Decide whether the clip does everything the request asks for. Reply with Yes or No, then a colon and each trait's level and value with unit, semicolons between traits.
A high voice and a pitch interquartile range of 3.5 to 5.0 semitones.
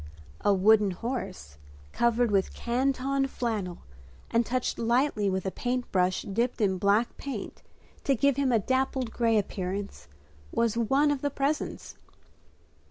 Yes: high, 235 Hz; average, 4.6 semitones